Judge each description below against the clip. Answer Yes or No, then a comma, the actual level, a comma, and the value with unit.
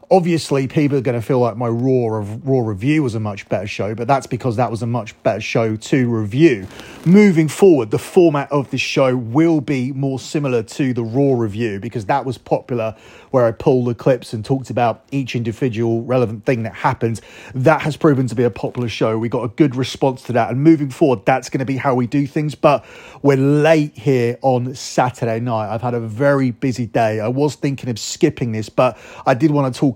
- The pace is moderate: No, fast, 220 wpm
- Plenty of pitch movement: No, average, 3.3 semitones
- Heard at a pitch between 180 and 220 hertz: No, low, 130 Hz